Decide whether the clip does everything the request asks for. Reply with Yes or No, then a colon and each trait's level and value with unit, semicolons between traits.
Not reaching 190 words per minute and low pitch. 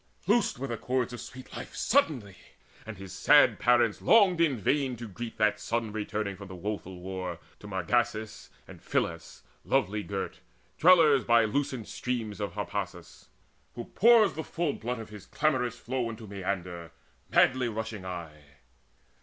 Yes: average, 155 wpm; low, 110 Hz